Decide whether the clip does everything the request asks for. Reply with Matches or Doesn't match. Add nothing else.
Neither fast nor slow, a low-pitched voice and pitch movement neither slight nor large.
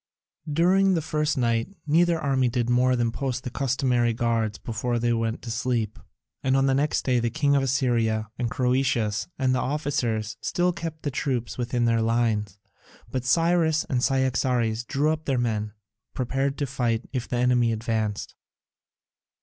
Matches